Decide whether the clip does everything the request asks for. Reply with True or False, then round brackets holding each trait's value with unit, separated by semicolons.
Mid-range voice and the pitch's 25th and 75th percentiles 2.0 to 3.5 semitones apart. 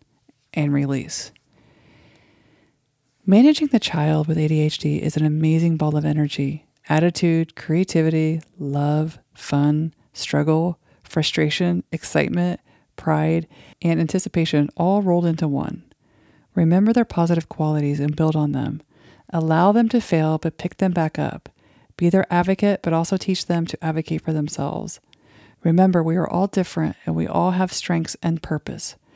True (160 Hz; 2.6 semitones)